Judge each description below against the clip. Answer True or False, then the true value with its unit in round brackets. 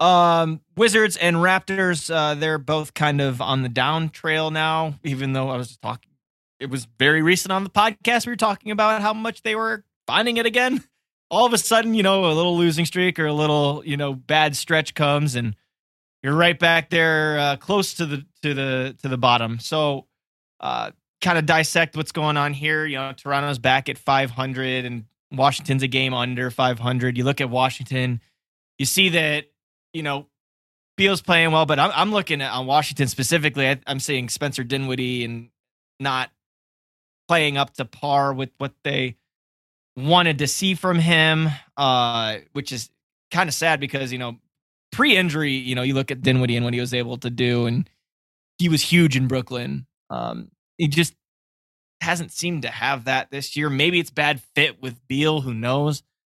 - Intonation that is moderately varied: True (4.2 semitones)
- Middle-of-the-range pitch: True (145 Hz)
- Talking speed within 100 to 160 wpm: False (190 wpm)